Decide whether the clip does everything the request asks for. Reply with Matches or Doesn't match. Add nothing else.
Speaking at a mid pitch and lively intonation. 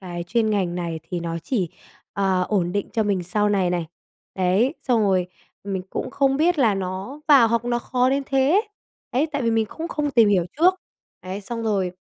Doesn't match